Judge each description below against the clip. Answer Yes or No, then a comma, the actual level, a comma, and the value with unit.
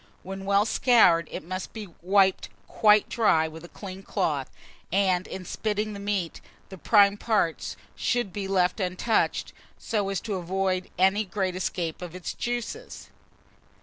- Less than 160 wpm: Yes, average, 150 wpm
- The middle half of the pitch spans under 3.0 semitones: Yes, narrow, 2.4 semitones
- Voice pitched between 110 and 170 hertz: No, high, 195 Hz